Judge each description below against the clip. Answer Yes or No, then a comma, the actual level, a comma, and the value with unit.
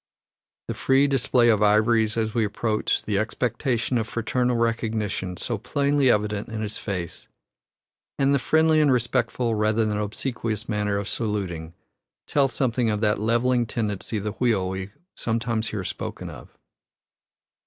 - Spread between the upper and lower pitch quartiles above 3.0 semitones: No, average, 2.7 semitones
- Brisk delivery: No, average, 150 wpm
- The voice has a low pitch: Yes, low, 110 Hz